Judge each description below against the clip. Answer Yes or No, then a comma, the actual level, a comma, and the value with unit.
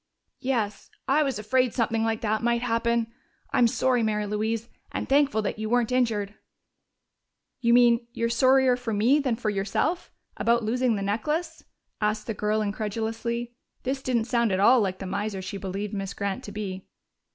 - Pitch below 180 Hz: No, high, 225 Hz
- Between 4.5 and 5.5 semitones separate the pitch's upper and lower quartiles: No, average, 2.8 semitones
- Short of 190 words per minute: Yes, average, 175 wpm